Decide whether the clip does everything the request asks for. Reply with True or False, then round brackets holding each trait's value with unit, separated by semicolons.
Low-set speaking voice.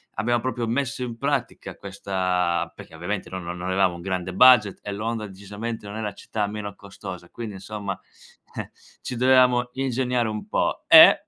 True (105 Hz)